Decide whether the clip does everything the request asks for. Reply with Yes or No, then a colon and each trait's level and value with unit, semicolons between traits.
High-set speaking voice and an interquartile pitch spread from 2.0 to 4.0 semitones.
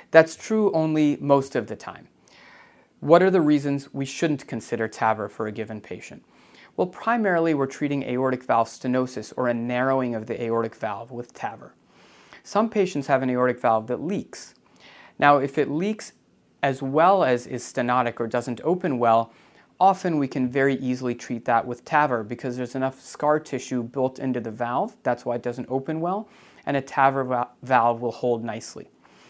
No: low, 130 Hz; average, 3.3 semitones